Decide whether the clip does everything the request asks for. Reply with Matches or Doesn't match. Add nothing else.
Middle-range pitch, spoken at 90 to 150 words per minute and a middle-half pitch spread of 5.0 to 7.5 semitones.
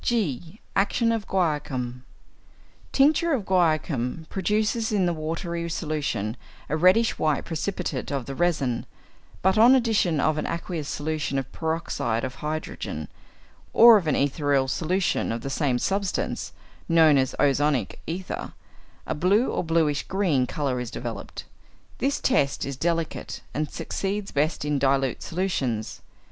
Matches